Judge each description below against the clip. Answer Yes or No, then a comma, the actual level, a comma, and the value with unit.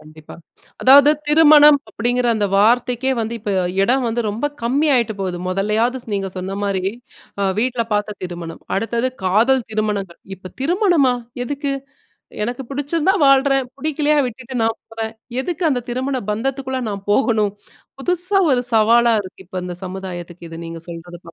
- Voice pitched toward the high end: Yes, high, 235 Hz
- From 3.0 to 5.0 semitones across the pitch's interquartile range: No, wide, 5.4 semitones